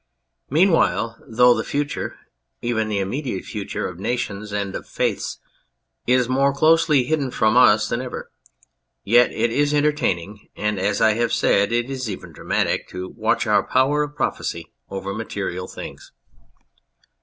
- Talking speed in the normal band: Yes, average, 150 wpm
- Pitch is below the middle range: Yes, low, 115 Hz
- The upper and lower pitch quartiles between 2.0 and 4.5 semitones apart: No, average, 5.0 semitones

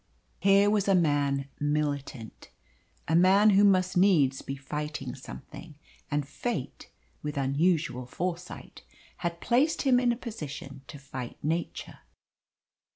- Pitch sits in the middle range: Yes, medium, 155 Hz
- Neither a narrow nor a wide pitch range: No, wide, 5.7 semitones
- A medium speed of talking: No, slow, 125 wpm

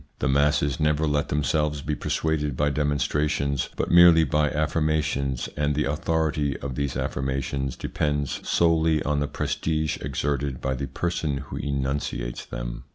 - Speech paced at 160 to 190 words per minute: No, average, 150 wpm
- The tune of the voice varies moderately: No, narrow, 1.9 semitones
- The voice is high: No, very low, 75 Hz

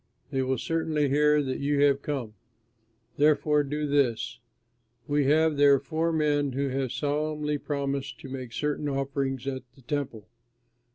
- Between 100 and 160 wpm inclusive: Yes, average, 150 wpm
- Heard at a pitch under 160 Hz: Yes, medium, 140 Hz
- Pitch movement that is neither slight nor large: No, narrow, 1.8 semitones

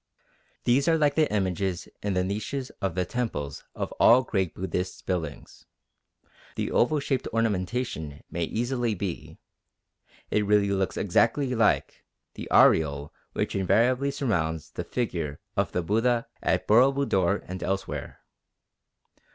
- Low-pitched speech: Yes, low, 100 Hz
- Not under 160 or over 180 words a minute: No, slow, 135 wpm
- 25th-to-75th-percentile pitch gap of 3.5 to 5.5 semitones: Yes, average, 5.2 semitones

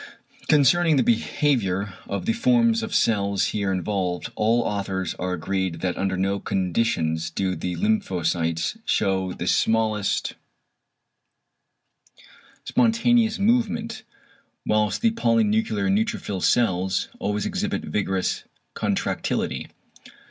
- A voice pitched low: Yes, low, 105 Hz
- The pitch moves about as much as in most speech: No, wide, 7.5 semitones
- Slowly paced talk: Yes, slow, 105 wpm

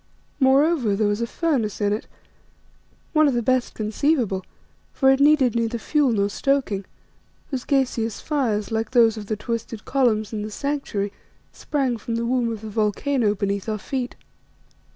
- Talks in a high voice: Yes, high, 230 Hz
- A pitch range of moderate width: Yes, average, 4.1 semitones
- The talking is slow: No, average, 165 wpm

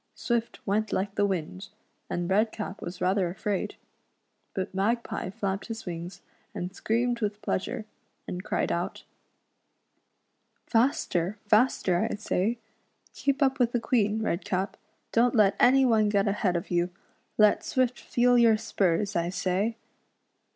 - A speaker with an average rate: Yes, average, 145 wpm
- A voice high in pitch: Yes, high, 210 Hz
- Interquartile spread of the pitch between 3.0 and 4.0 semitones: Yes, average, 3.7 semitones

